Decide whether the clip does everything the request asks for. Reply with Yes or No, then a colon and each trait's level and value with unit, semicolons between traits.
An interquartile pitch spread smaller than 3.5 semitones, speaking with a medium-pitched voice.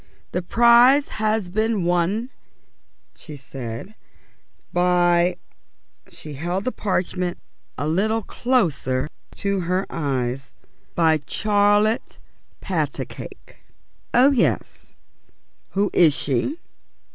No: wide, 5.4 semitones; medium, 180 Hz